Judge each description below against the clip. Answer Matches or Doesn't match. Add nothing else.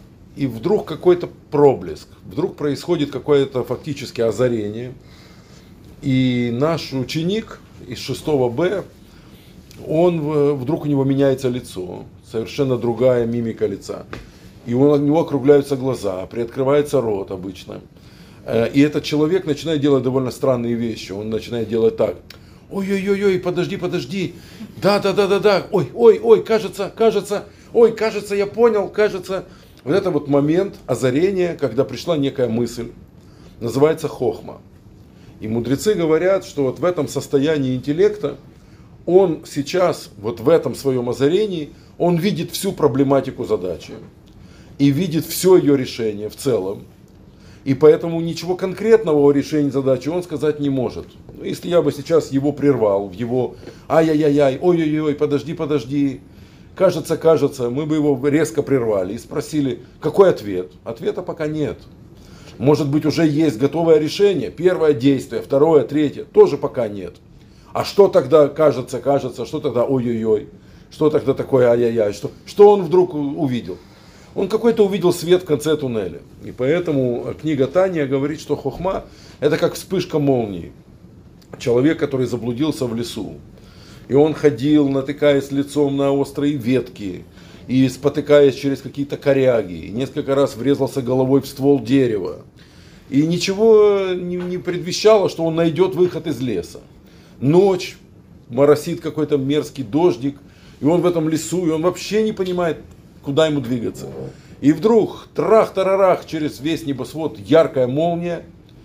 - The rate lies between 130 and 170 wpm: Matches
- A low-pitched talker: Doesn't match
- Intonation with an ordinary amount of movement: Matches